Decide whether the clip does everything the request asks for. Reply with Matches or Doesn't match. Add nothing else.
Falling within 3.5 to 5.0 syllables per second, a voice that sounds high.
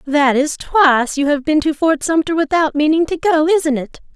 Matches